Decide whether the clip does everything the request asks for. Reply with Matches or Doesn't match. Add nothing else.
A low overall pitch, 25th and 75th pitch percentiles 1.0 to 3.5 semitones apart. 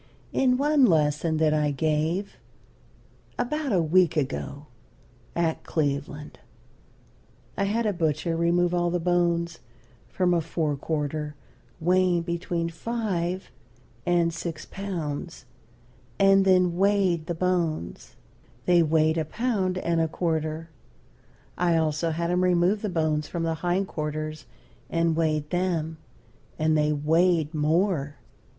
Doesn't match